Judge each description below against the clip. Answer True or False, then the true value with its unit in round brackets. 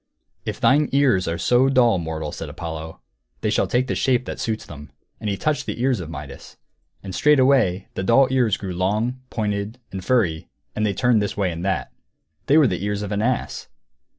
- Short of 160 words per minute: False (205 wpm)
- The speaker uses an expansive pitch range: True (5.8 semitones)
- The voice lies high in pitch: False (105 Hz)